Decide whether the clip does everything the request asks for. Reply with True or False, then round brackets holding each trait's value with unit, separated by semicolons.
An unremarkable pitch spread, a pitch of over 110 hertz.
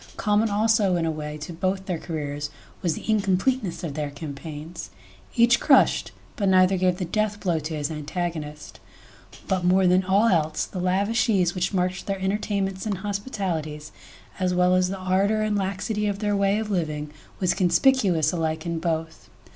True (3.8 semitones; 185 Hz)